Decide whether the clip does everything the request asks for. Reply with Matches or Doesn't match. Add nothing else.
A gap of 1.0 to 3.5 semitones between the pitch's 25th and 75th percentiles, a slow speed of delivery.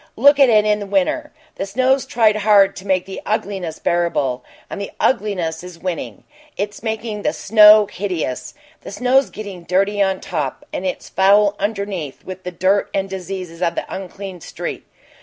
Doesn't match